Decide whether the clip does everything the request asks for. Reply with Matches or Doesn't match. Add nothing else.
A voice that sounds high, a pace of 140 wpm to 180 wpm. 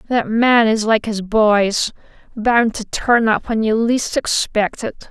Matches